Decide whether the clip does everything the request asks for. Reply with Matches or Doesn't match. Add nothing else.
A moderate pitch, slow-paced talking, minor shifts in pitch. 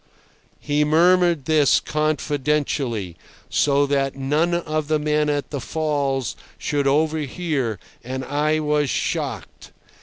Matches